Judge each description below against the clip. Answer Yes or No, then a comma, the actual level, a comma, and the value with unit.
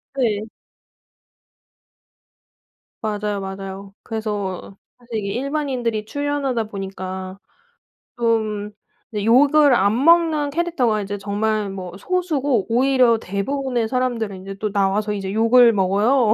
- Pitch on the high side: Yes, high, 220 Hz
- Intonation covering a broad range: No, average, 4.4 semitones